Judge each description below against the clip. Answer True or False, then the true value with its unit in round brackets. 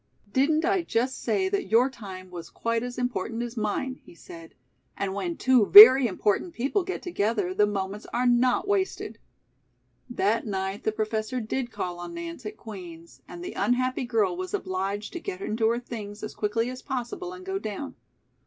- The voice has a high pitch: True (230 Hz)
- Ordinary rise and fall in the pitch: True (4.4 semitones)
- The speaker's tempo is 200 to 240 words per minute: False (180 wpm)